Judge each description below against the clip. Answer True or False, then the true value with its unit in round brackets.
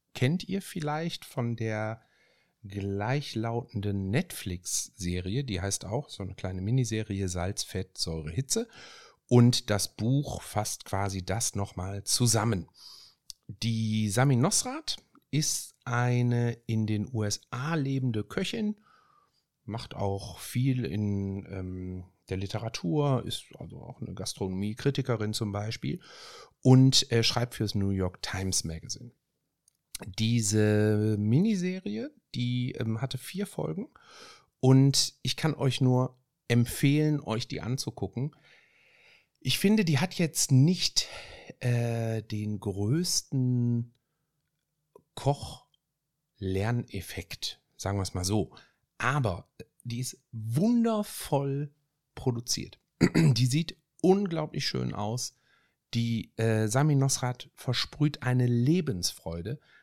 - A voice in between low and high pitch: False (120 Hz)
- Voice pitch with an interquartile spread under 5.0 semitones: False (5.6 semitones)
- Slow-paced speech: True (105 wpm)